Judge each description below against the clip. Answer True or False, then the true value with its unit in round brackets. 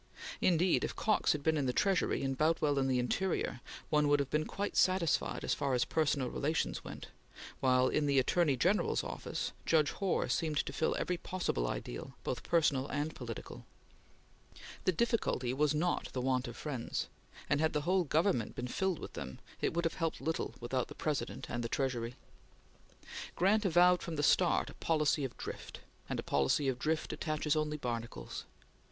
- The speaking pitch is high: False (150 Hz)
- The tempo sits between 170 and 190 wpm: True (185 wpm)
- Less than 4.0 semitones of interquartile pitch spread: False (4.4 semitones)